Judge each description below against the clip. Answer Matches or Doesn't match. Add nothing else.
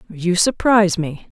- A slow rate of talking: Matches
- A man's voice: Doesn't match